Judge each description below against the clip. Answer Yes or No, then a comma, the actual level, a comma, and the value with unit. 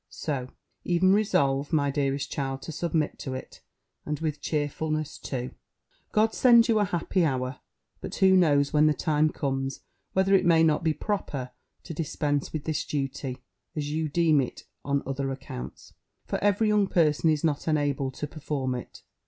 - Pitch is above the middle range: No, medium, 150 Hz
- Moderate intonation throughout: Yes, average, 3.3 semitones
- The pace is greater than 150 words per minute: Yes, average, 170 wpm